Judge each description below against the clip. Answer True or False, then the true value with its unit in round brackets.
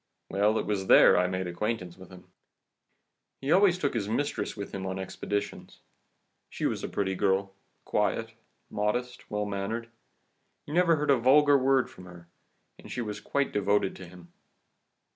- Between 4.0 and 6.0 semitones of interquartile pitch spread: True (5.5 semitones)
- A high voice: False (105 Hz)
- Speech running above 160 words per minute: True (170 wpm)